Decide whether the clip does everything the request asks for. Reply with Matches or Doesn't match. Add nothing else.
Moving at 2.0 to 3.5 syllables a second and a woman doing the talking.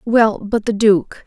Matches